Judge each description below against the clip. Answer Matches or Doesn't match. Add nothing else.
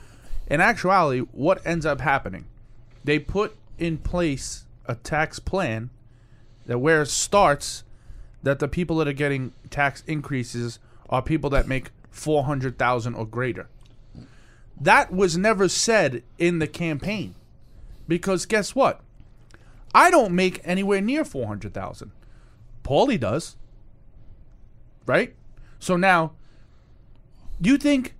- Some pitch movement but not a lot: Doesn't match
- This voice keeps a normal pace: Doesn't match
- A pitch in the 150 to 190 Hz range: Doesn't match